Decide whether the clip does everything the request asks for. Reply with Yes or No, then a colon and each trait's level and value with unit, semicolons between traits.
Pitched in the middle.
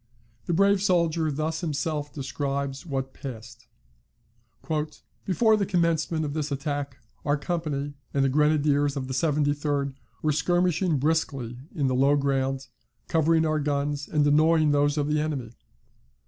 Yes: medium, 145 Hz